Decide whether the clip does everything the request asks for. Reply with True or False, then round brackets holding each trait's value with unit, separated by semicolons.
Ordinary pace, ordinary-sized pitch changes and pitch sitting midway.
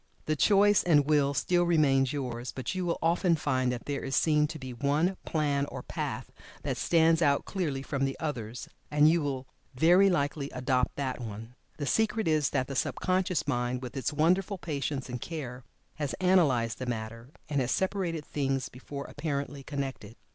True (185 wpm; 4.0 semitones; 145 Hz)